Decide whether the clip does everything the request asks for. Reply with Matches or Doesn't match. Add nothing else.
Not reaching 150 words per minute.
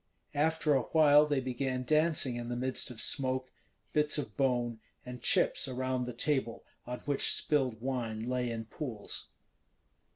Doesn't match